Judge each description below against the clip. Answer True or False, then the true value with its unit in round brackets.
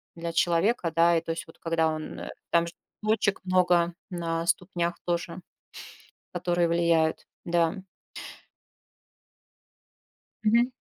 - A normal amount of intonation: False (1.3 semitones)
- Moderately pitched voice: True (170 Hz)